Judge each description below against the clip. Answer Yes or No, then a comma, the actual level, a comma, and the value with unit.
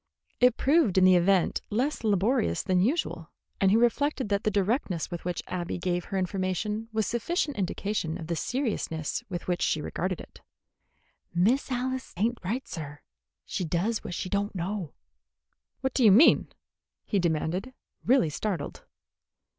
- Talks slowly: No, average, 155 wpm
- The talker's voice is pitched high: Yes, high, 200 Hz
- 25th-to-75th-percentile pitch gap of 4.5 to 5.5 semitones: Yes, average, 5.1 semitones